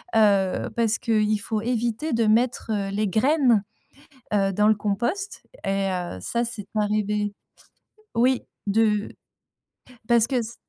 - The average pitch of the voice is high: Yes, high, 215 Hz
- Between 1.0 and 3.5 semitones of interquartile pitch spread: Yes, narrow, 2.4 semitones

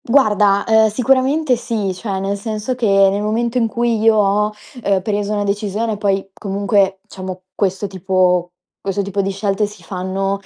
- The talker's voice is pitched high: Yes, high, 205 Hz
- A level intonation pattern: Yes, narrow, 2.2 semitones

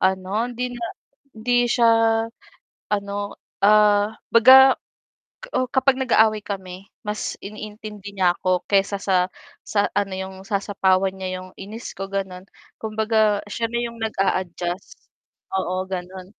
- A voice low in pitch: No, high, 205 Hz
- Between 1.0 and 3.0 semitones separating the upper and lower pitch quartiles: Yes, narrow, 2.5 semitones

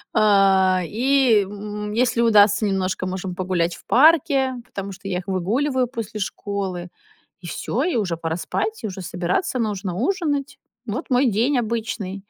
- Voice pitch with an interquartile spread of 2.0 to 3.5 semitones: No, average, 4.8 semitones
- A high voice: Yes, high, 210 Hz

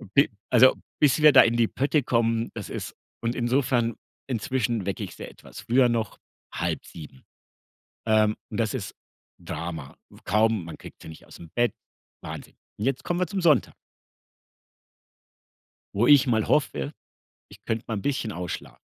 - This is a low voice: Yes, low, 115 Hz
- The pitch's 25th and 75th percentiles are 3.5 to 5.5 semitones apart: Yes, average, 3.9 semitones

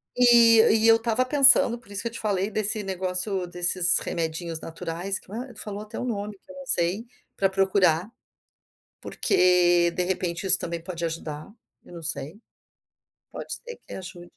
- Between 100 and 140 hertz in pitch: No, high, 190 Hz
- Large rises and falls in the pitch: No, average, 4.1 semitones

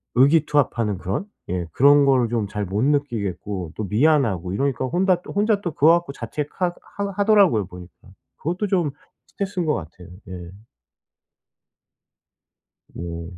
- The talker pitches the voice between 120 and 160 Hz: Yes, low, 135 Hz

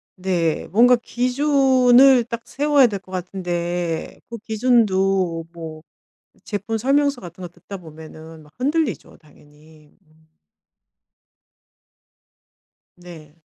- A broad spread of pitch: Yes, wide, 6.9 semitones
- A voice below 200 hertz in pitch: Yes, high, 190 Hz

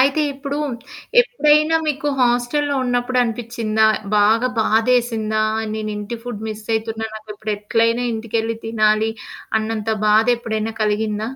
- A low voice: No, high, 225 Hz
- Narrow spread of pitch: Yes, narrow, 2.2 semitones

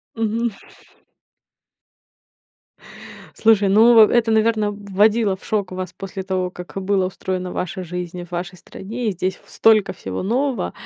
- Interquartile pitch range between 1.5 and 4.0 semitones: Yes, average, 3.2 semitones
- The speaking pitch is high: Yes, high, 195 Hz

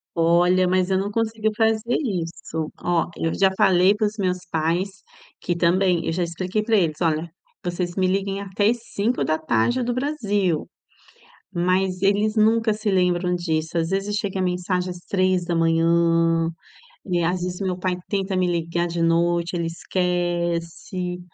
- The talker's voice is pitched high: No, medium, 180 Hz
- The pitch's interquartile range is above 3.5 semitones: No, narrow, 2.5 semitones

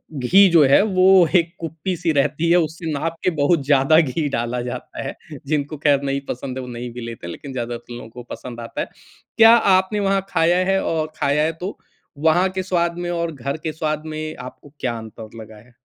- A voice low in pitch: No, medium, 155 Hz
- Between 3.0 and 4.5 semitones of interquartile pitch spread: No, average, 5.2 semitones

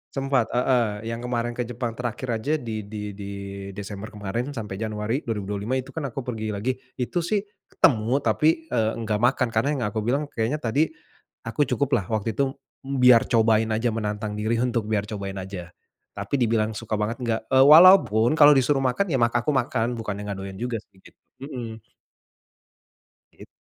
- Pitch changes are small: No, average, 3.2 semitones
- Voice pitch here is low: Yes, low, 115 Hz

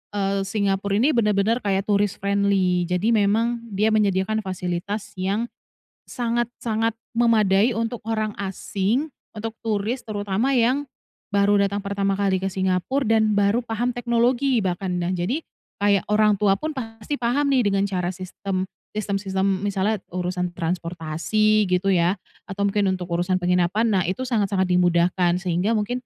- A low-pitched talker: No, high, 200 Hz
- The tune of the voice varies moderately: Yes, average, 3.0 semitones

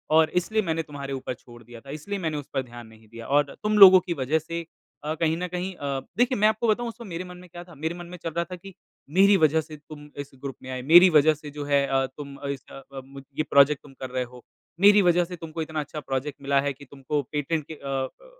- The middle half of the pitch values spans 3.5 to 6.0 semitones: Yes, average, 4.2 semitones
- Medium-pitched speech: Yes, medium, 150 Hz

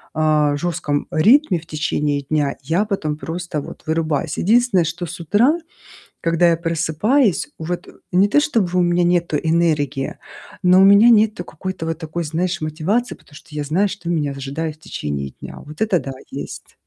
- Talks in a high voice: No, medium, 165 Hz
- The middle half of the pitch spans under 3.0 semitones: No, average, 3.5 semitones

